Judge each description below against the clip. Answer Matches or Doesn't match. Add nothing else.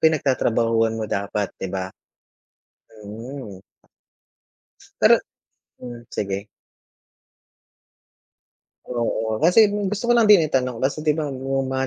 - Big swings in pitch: Matches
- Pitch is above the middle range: Doesn't match